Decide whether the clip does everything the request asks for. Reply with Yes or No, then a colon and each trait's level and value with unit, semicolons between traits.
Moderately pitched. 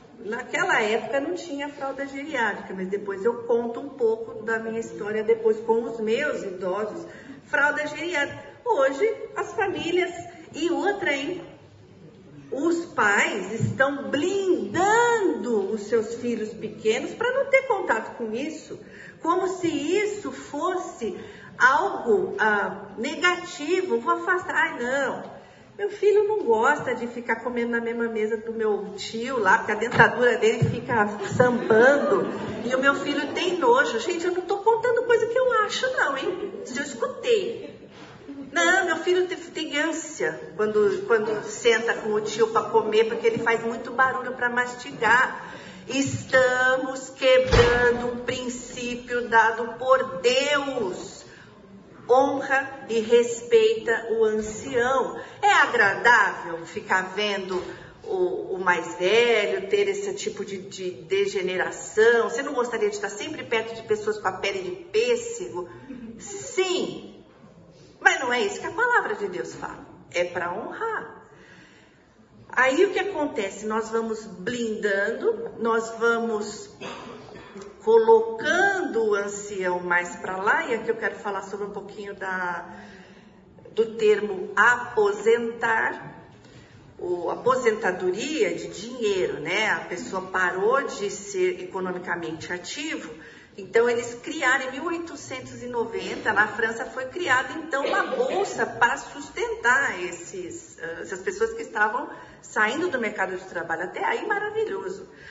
No: very high, 260 Hz